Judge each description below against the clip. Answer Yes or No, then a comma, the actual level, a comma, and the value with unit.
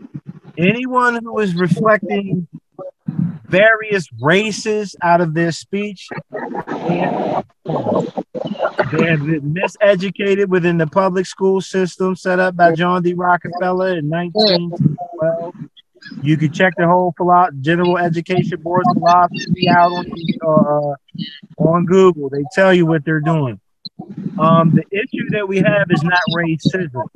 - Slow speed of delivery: Yes, slow, 125 wpm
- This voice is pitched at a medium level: Yes, medium, 180 Hz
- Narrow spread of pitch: Yes, narrow, 2.2 semitones